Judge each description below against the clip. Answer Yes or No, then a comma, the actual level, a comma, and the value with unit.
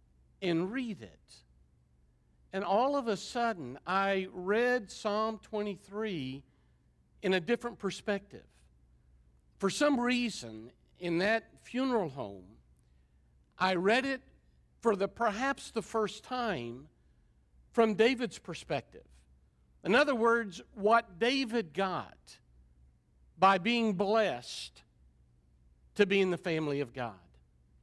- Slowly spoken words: Yes, slow, 110 wpm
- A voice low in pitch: No, high, 190 Hz